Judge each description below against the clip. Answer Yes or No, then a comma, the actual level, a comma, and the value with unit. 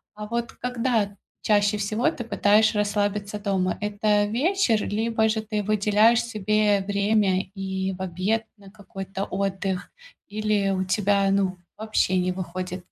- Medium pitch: No, high, 205 Hz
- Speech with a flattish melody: Yes, narrow, 1.9 semitones